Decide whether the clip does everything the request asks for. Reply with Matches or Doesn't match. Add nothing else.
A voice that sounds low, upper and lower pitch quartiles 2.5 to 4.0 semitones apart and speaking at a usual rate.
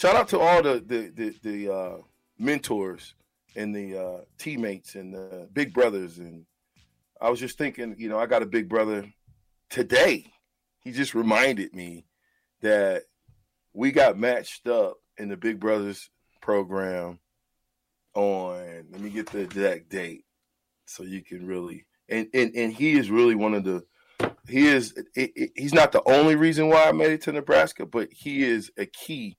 Doesn't match